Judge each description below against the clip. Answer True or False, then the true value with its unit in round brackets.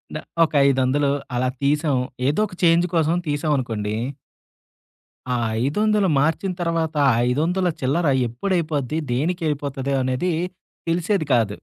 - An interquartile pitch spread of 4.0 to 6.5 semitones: True (4.4 semitones)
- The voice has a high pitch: False (150 Hz)